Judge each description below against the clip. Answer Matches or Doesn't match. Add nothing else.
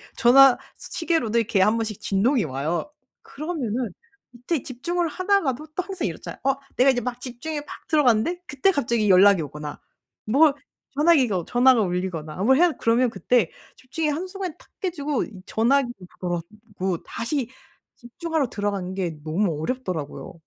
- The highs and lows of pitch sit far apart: Matches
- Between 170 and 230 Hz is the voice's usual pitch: Doesn't match